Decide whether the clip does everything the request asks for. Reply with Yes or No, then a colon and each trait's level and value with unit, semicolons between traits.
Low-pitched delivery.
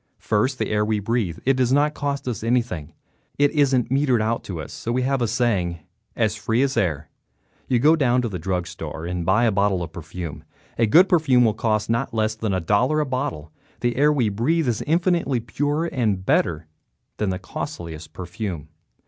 Yes: low, 115 Hz